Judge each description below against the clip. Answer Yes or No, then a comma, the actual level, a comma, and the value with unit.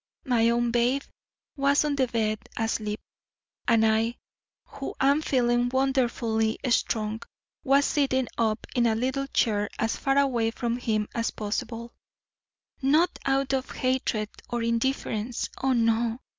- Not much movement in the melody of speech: No, average, 3.0 semitones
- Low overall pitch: No, high, 240 Hz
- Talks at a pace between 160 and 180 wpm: No, slow, 135 wpm